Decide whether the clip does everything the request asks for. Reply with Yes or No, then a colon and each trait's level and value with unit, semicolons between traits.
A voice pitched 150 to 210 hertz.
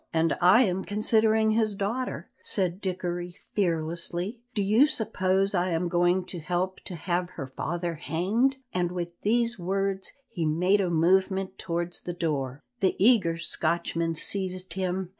Yes: medium, 185 Hz